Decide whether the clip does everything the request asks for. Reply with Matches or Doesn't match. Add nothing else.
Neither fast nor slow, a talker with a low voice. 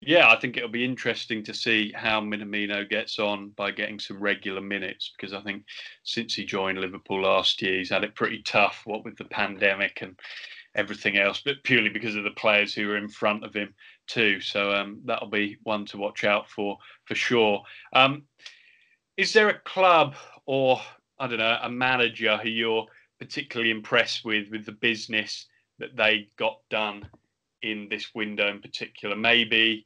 Matches